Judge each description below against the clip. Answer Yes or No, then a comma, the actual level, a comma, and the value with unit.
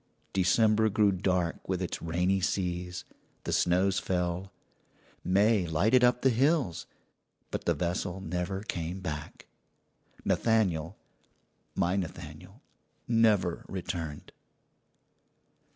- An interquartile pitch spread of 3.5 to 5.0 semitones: No, average, 3.0 semitones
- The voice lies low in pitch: Yes, very low, 95 Hz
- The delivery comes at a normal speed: No, slow, 100 wpm